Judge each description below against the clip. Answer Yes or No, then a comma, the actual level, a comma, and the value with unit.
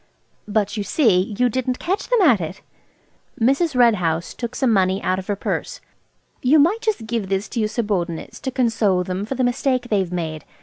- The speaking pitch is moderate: No, high, 220 Hz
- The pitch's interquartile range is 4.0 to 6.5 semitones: Yes, average, 5.2 semitones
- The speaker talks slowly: No, average, 200 wpm